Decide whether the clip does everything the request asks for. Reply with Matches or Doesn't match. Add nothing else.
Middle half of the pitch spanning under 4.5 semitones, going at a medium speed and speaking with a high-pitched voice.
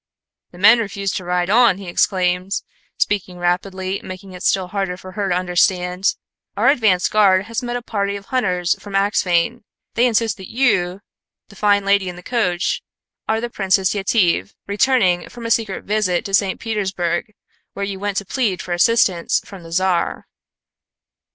Matches